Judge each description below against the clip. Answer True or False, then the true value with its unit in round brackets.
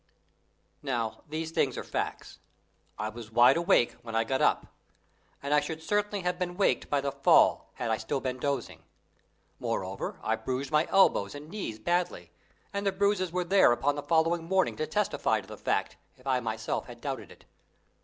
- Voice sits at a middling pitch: True (145 Hz)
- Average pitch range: False (6.8 semitones)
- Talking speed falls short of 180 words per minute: False (185 wpm)